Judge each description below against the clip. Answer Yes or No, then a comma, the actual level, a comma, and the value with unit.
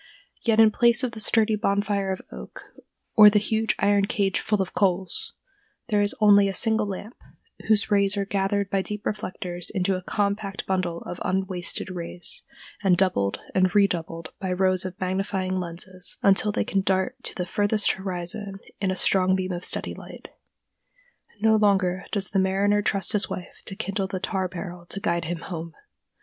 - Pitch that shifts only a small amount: Yes, narrow, 1.9 semitones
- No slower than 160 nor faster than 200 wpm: Yes, average, 180 wpm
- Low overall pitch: No, high, 195 Hz